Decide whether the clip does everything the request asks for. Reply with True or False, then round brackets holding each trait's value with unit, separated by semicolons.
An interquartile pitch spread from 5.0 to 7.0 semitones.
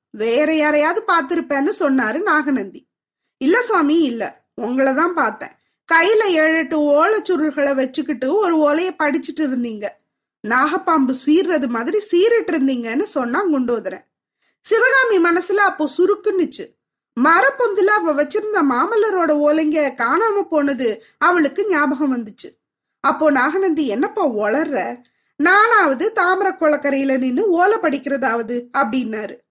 True (5.3 semitones)